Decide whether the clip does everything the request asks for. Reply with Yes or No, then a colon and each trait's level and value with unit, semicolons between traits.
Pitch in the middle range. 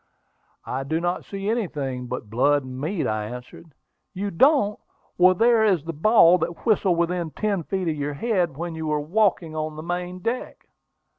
Yes: medium, 170 Hz